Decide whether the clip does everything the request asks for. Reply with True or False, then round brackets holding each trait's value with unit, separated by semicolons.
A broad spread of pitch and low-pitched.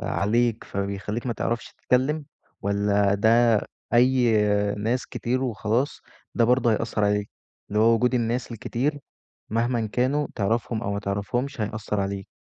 False (3.1 semitones; 115 Hz)